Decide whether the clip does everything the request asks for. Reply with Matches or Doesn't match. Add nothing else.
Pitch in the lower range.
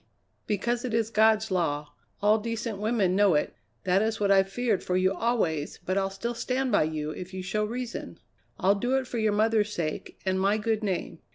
Doesn't match